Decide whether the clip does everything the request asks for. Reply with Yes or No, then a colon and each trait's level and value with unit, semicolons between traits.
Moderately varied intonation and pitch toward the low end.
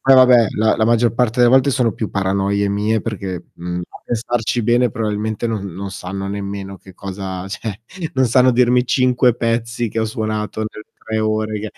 Yes: average, 3.1 semitones; low, 110 Hz